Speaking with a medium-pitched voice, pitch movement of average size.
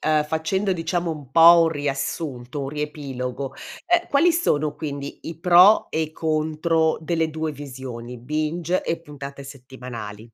Yes: medium, 155 Hz; average, 3.1 semitones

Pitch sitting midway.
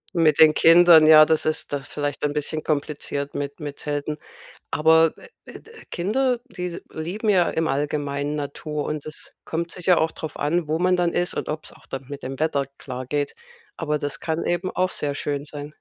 Yes: medium, 155 Hz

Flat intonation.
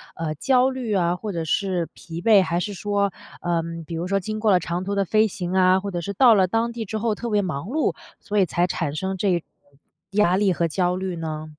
No: average, 3.3 semitones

